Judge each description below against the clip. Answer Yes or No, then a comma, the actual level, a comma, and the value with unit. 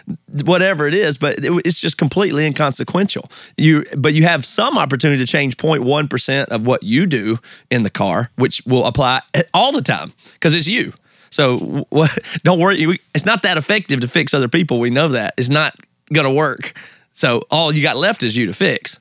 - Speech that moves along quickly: No, average, 195 wpm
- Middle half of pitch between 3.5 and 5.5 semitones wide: Yes, average, 4.2 semitones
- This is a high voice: No, medium, 155 Hz